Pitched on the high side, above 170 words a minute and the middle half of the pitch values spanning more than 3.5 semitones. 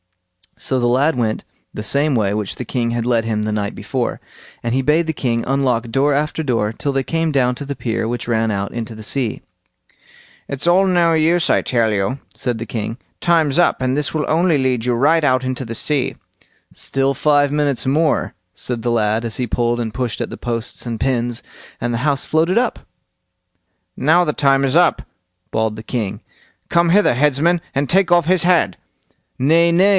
No: low, 130 Hz; average, 200 wpm; average, 4.7 semitones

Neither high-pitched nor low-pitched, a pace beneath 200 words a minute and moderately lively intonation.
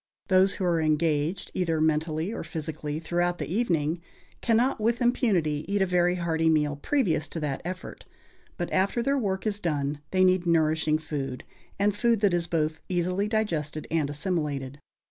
Yes: medium, 170 Hz; average, 165 wpm; average, 3.8 semitones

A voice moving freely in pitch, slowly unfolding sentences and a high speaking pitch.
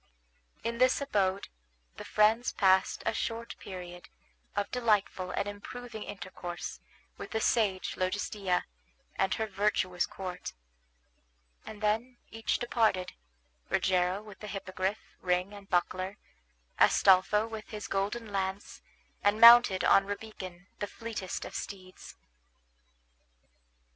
No: average, 2.8 semitones; slow, 115 wpm; high, 200 Hz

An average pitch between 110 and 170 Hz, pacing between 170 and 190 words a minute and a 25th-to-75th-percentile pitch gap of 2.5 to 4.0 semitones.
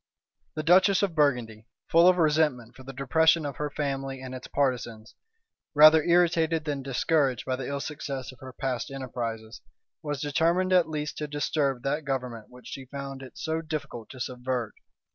Yes: medium, 140 Hz; average, 175 wpm; average, 3.5 semitones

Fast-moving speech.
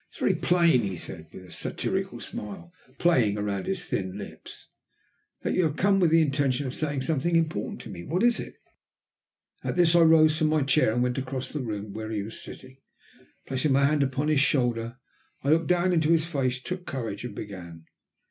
Yes: fast, 210 wpm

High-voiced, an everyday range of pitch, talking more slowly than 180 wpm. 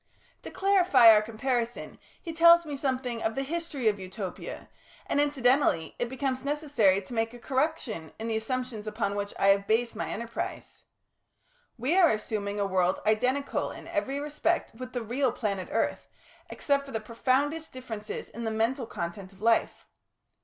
Yes: high, 240 Hz; average, 4.6 semitones; average, 165 wpm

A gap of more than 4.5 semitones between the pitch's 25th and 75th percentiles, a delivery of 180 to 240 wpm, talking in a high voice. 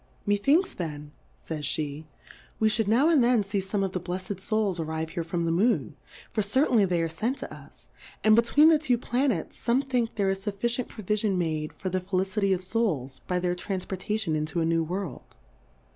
Yes: average, 5.1 semitones; average, 195 wpm; high, 195 Hz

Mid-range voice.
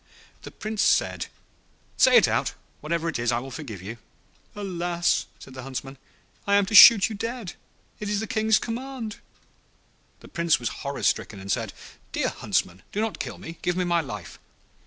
Yes: medium, 170 Hz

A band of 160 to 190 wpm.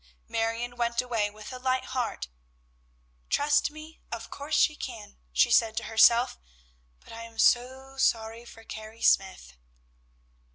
No: average, 140 wpm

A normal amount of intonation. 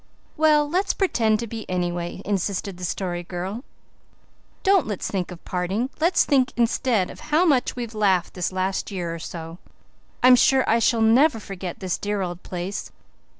No: wide, 5.8 semitones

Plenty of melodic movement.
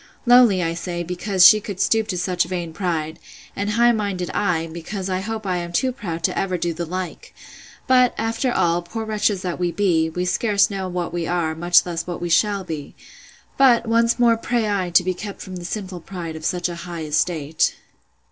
No: average, 3.4 semitones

